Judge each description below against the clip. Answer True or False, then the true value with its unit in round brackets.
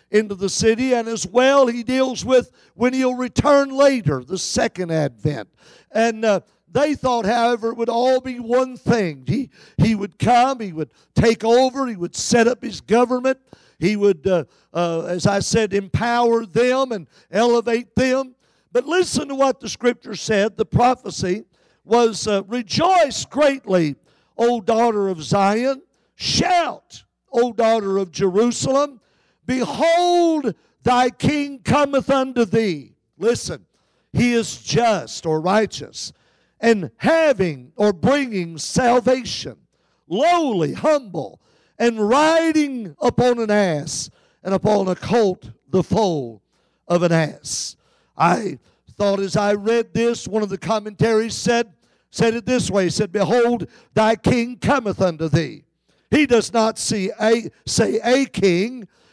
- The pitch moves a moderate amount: True (4.4 semitones)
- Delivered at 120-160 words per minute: True (140 wpm)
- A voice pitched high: True (230 Hz)